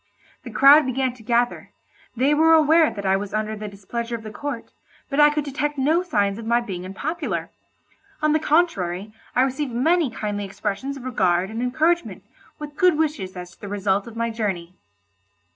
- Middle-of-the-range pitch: No, high, 240 Hz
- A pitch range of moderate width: No, wide, 6.4 semitones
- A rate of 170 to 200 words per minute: Yes, average, 190 wpm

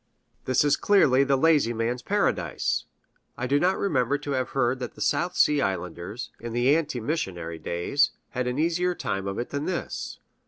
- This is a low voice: Yes, low, 130 Hz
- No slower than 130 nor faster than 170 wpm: No, average, 185 wpm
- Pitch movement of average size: Yes, average, 4.3 semitones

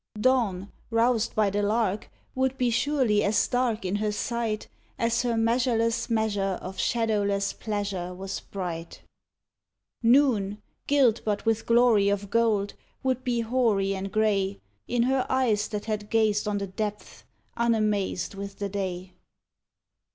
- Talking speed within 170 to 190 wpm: No, average, 140 wpm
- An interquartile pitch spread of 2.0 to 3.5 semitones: Yes, average, 2.8 semitones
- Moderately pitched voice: No, high, 215 Hz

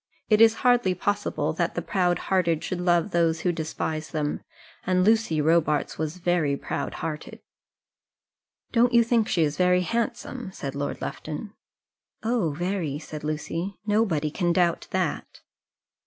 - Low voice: No, medium, 175 Hz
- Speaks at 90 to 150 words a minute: Yes, average, 145 wpm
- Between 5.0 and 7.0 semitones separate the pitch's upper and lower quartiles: No, average, 4.6 semitones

